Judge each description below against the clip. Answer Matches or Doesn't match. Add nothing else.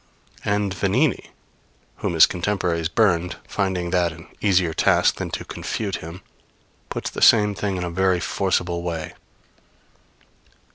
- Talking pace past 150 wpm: Doesn't match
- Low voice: Matches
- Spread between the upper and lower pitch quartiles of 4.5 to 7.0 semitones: Doesn't match